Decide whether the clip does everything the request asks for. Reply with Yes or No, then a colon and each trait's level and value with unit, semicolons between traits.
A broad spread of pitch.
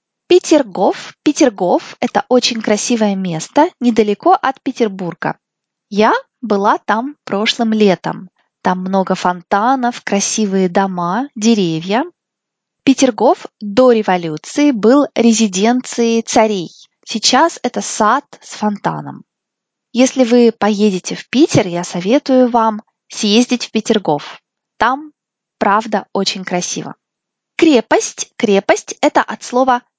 No: average, 4.4 semitones